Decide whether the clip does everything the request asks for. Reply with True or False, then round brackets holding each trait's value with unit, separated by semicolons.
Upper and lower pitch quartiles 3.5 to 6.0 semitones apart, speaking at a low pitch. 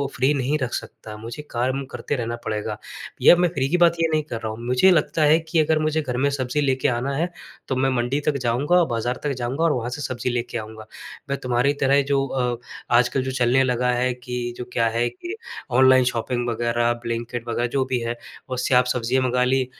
False (2.7 semitones; 125 Hz)